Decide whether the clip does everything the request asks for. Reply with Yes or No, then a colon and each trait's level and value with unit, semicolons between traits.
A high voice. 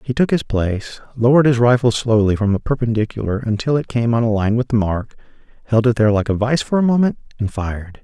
No: low, 115 Hz